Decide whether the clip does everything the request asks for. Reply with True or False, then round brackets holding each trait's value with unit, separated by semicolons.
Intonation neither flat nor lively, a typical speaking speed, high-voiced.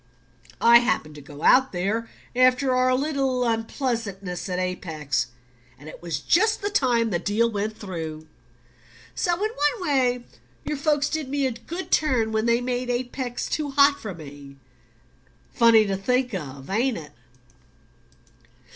False (6.3 semitones; 150 wpm; 235 Hz)